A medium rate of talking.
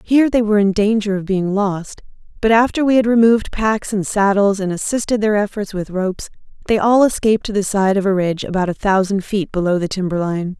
No: fast, 215 wpm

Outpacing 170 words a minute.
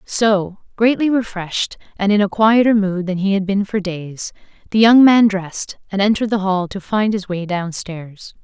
Yes: average, 190 wpm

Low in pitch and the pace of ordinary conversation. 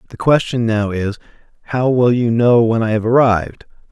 Yes: low, 115 Hz; average, 185 wpm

